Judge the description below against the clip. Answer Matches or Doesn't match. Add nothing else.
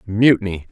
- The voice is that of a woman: Doesn't match